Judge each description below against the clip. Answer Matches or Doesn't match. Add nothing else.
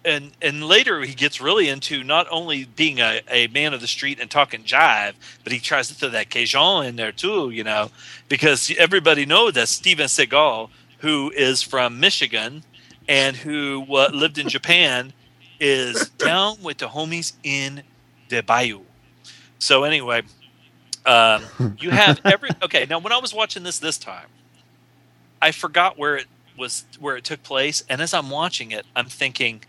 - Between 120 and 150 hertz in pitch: Matches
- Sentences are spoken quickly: Doesn't match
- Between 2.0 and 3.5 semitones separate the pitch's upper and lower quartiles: Doesn't match